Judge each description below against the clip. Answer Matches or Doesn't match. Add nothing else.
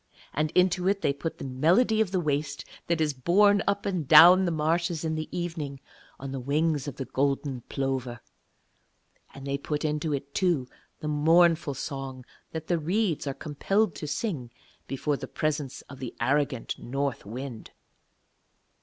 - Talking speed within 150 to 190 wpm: Matches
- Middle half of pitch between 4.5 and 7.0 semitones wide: Doesn't match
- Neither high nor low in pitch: Matches